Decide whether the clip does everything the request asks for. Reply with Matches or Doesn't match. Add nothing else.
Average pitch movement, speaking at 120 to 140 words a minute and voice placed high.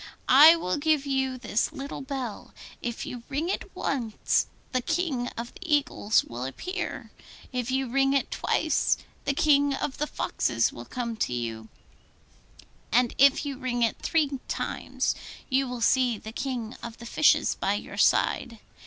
Doesn't match